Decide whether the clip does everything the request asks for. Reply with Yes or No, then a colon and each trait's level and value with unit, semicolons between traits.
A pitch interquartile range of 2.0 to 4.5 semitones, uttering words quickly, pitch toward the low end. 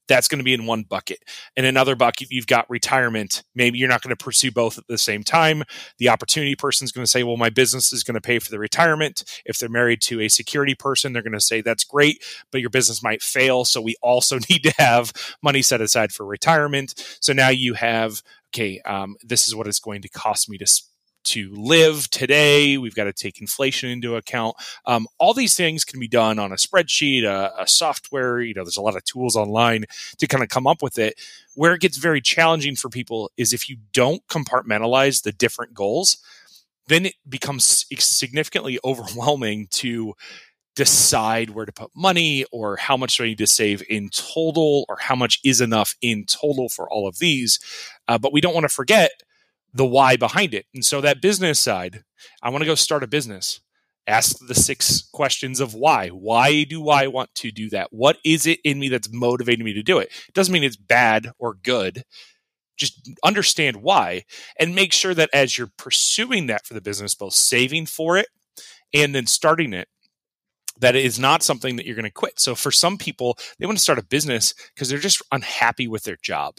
Yes: average, 4.1 semitones; fast, 215 wpm; low, 125 Hz